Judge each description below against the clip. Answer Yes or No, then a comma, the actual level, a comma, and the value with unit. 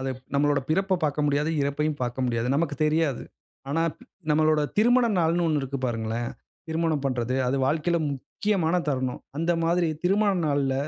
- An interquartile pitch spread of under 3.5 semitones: No, average, 3.9 semitones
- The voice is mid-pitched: Yes, medium, 150 Hz